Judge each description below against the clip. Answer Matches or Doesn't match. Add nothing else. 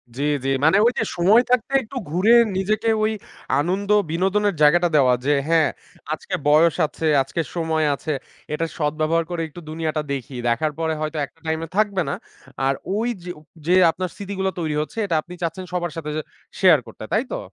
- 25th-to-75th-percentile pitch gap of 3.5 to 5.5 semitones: Matches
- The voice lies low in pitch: Doesn't match